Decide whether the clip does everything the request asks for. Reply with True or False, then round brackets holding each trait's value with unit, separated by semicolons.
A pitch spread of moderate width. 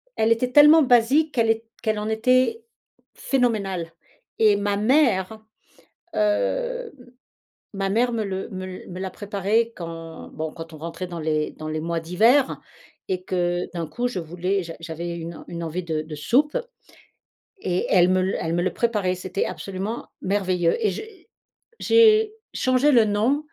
False (6.0 semitones)